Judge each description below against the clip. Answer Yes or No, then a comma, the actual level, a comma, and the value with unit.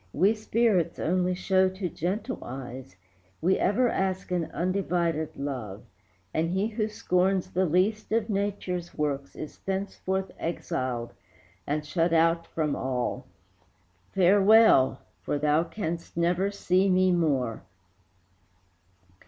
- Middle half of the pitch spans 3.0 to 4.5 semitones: Yes, average, 4.0 semitones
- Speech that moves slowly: Yes, slow, 120 wpm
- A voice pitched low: No, medium, 180 Hz